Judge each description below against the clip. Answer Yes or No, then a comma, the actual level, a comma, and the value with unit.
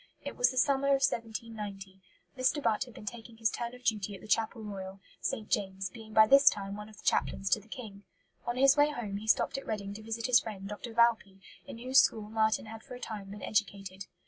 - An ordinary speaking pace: No, fast, 235 wpm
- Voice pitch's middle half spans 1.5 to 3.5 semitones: Yes, average, 2.9 semitones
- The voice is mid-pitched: No, high, 220 Hz